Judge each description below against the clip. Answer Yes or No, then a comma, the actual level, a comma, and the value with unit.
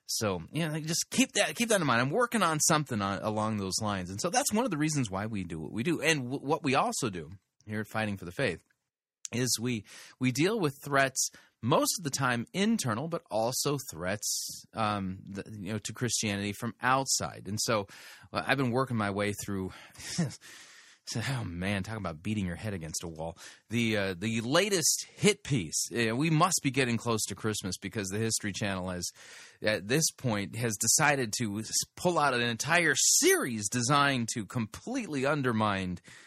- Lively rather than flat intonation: Yes, wide, 5.8 semitones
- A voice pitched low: Yes, low, 115 Hz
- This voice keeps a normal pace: Yes, average, 195 wpm